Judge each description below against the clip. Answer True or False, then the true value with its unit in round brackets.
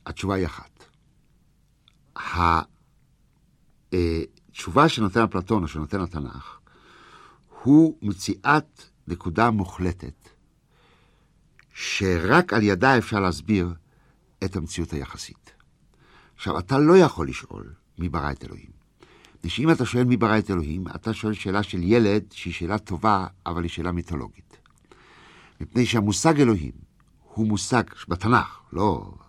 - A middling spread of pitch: True (4.8 semitones)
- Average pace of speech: True (115 wpm)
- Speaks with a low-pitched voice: True (100 Hz)